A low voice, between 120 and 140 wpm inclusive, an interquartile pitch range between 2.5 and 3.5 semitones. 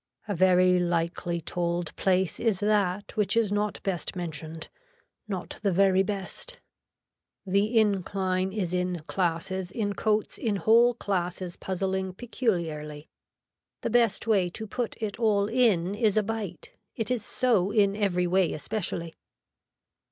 No: high, 190 Hz; slow, 135 wpm; average, 3.2 semitones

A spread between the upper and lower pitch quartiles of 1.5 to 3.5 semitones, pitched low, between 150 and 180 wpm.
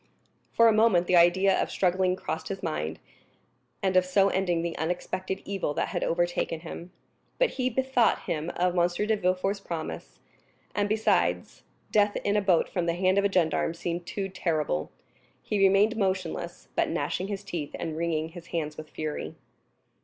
No: average, 2.9 semitones; medium, 180 Hz; average, 175 wpm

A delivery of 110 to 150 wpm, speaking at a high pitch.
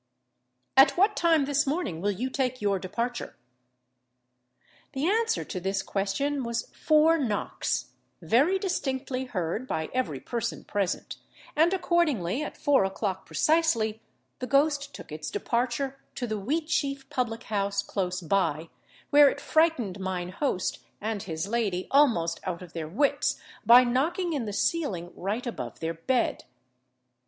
Yes: average, 145 wpm; high, 240 Hz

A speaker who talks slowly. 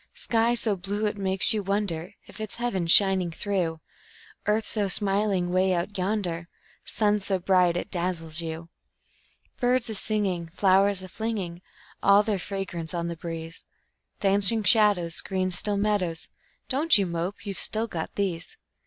No: average, 155 wpm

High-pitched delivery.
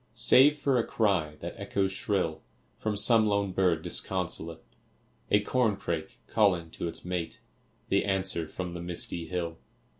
No: very low, 95 Hz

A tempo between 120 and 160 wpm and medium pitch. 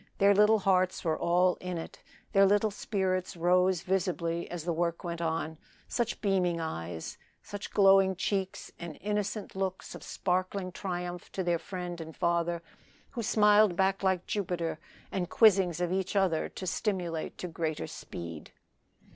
Yes: average, 155 wpm; medium, 180 Hz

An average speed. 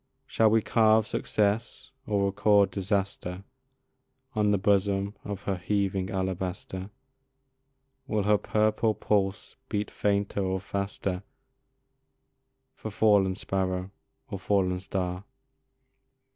No: slow, 105 wpm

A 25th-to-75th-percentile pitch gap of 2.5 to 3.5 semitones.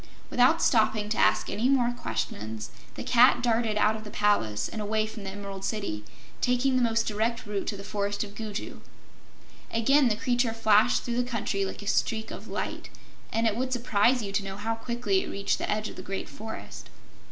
Yes: average, 2.8 semitones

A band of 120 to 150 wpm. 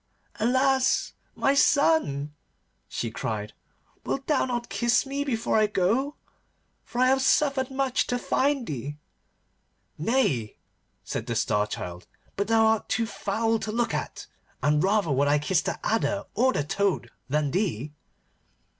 Yes: average, 145 wpm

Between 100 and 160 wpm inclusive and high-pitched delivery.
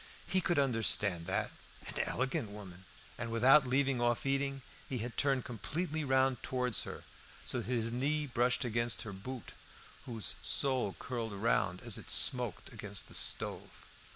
No: average, 155 wpm; low, 125 Hz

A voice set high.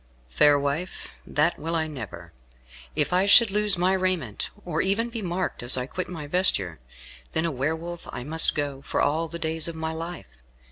No: medium, 160 Hz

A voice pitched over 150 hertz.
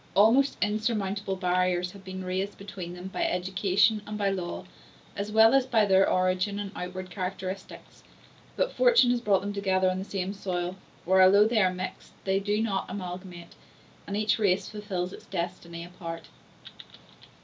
Yes: high, 190 Hz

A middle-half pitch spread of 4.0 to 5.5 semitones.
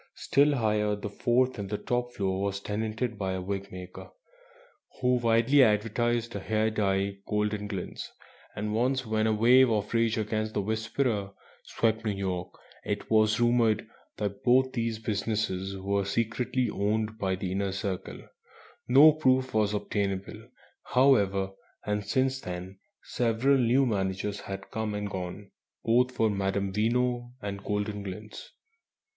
No: average, 3.1 semitones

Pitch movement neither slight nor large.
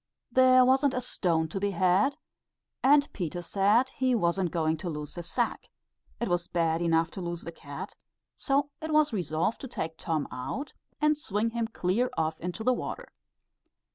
No: wide, 7.4 semitones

